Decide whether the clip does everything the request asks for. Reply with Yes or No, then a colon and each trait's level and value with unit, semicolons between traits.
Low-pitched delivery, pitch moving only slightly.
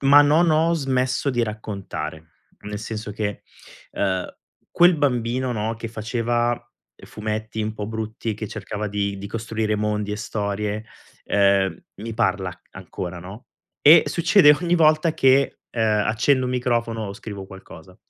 No: low, 110 Hz; average, 3.7 semitones